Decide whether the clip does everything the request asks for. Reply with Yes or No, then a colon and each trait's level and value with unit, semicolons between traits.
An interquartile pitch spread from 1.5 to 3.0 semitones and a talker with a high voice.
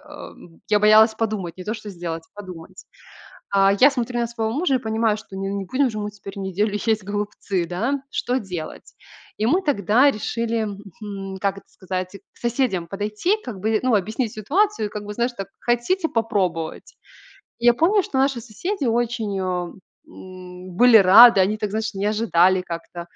No: average, 3.7 semitones; high, 210 Hz